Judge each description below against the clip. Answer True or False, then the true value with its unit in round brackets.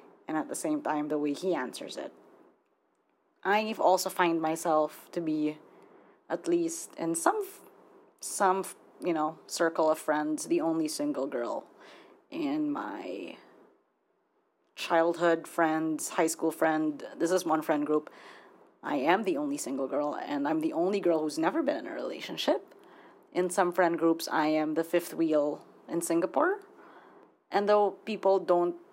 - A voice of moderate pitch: True (180 Hz)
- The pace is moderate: True (160 wpm)